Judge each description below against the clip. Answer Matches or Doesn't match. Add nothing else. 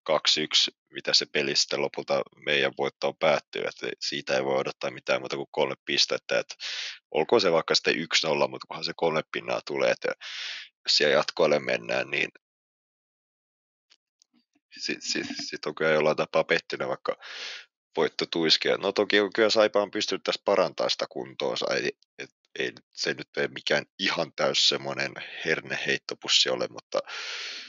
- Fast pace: Matches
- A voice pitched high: Matches